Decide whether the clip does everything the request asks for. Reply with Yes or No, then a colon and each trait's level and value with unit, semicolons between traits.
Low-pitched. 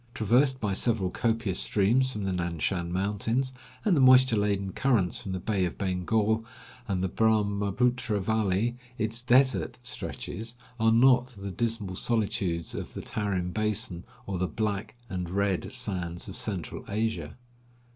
Yes: low, 105 Hz